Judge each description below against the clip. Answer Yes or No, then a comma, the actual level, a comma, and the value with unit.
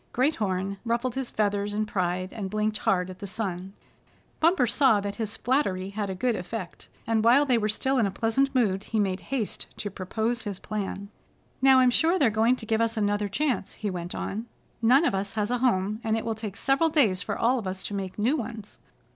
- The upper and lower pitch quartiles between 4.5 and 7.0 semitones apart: No, average, 3.7 semitones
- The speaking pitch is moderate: No, high, 215 Hz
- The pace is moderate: No, fast, 220 wpm